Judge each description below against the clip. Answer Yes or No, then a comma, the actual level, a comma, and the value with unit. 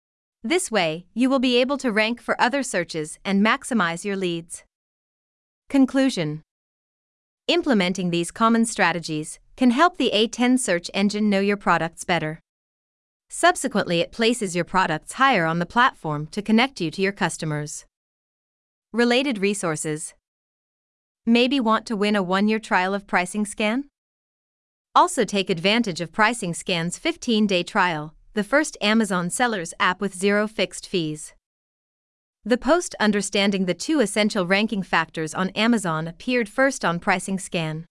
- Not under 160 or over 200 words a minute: No, average, 140 wpm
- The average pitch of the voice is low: No, high, 200 Hz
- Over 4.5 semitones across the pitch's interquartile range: Yes, average, 5.3 semitones